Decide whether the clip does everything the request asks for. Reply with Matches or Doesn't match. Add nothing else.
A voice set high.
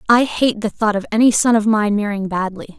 Matches